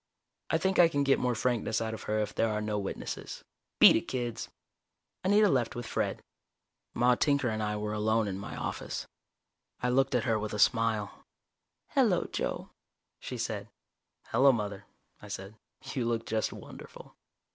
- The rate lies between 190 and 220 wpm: No, average, 170 wpm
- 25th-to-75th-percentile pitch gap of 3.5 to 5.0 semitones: No, average, 3.0 semitones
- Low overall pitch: Yes, low, 115 Hz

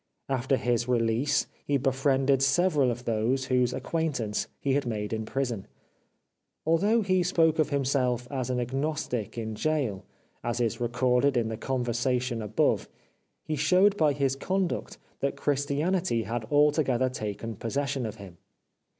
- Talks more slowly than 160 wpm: Yes, average, 140 wpm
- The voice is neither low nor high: No, low, 130 Hz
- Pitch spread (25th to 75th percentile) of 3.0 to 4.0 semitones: Yes, average, 3.6 semitones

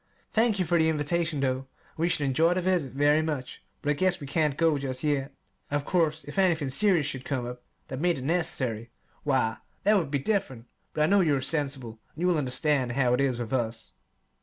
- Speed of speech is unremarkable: No, fast, 220 wpm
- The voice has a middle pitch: Yes, medium, 145 Hz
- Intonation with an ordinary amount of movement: Yes, average, 4.1 semitones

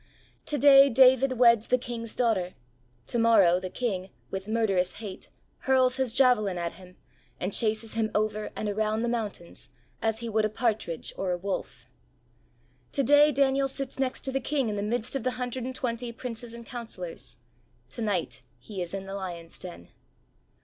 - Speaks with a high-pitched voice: Yes, high, 225 Hz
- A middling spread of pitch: Yes, average, 4.4 semitones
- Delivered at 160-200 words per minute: Yes, average, 180 wpm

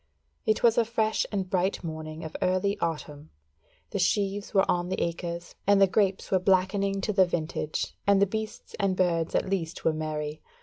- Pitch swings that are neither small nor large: Yes, average, 3.3 semitones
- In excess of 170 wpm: Yes, average, 185 wpm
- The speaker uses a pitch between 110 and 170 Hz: No, medium, 185 Hz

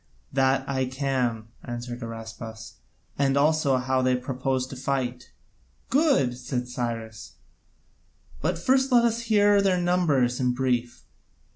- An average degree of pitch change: Yes, average, 4.0 semitones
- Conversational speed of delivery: No, slow, 125 wpm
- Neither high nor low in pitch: No, low, 130 Hz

